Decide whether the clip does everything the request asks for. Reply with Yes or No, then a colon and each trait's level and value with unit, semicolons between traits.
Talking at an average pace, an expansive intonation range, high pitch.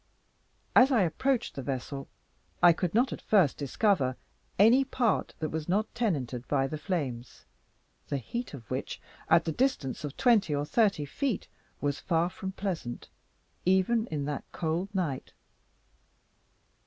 No: average, 145 wpm; wide, 7.2 semitones; medium, 170 Hz